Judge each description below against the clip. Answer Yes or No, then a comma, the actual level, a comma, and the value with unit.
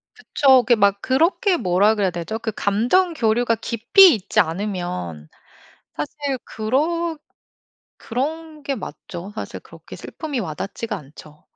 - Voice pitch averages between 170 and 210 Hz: No, high, 225 Hz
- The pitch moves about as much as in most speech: No, wide, 6.9 semitones